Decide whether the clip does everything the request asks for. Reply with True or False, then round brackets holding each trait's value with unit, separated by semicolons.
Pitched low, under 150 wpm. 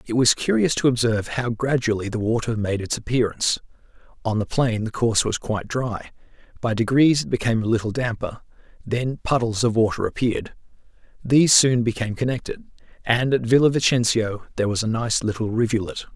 False (115 Hz; 170 wpm)